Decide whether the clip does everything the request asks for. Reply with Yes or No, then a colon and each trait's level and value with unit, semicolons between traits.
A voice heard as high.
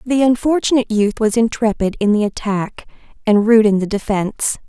Yes: high, 220 Hz